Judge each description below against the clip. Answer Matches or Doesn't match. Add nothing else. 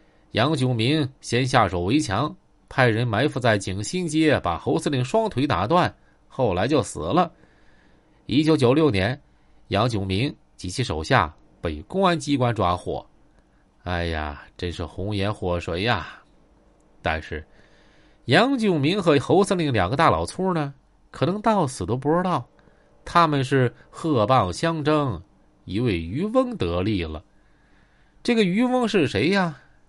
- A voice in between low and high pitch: Doesn't match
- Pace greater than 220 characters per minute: Doesn't match